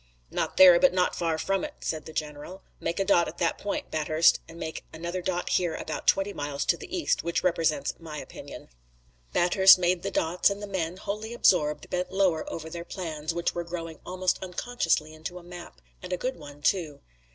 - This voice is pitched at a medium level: Yes, medium, 175 Hz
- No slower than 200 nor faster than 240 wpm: Yes, fast, 205 wpm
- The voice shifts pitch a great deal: No, average, 2.8 semitones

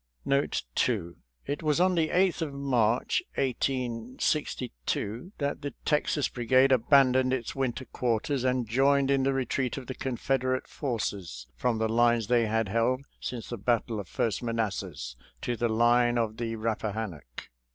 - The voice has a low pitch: Yes, low, 120 Hz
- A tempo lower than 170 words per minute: Yes, average, 155 wpm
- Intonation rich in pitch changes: No, average, 3.2 semitones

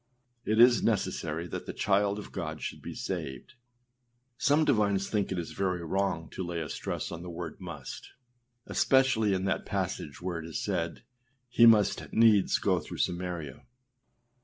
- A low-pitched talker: Yes, very low, 95 Hz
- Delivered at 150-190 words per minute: Yes, average, 165 wpm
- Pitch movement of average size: Yes, average, 4.0 semitones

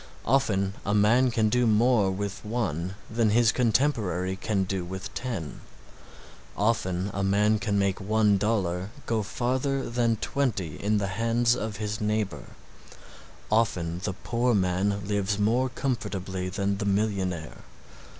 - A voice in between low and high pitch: No, low, 105 Hz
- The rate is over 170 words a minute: No, average, 140 wpm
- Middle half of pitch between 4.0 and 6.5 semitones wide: No, average, 3.1 semitones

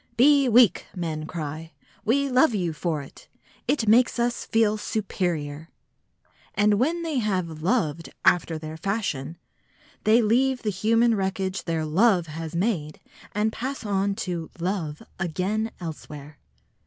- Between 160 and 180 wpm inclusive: No, slow, 135 wpm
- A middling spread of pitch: No, wide, 5.9 semitones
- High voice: Yes, high, 195 Hz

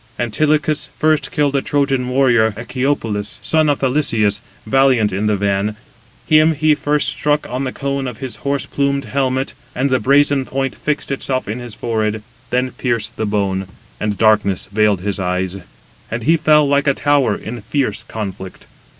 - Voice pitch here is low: Yes, low, 130 Hz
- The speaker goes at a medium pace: Yes, average, 165 wpm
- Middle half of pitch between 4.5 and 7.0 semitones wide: Yes, average, 4.8 semitones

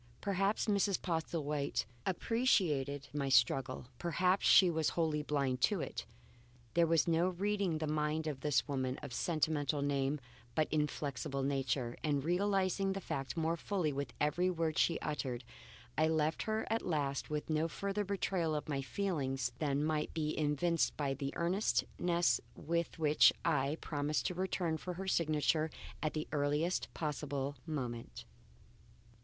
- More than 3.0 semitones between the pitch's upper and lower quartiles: Yes, average, 3.5 semitones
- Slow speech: No, average, 150 wpm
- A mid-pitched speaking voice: Yes, medium, 155 Hz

